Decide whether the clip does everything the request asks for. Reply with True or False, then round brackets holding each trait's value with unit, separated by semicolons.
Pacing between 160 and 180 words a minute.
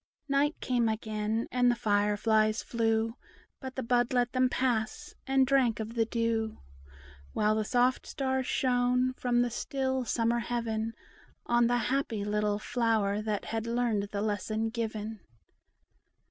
False (145 wpm)